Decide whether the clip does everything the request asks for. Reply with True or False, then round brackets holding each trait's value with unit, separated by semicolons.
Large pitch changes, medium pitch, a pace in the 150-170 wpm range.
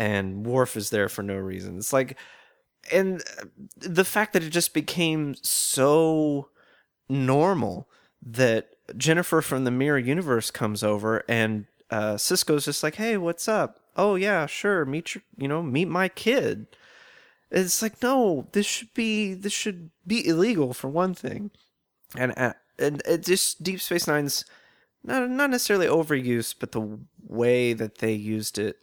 True (7.8 semitones; 150 Hz; 160 wpm)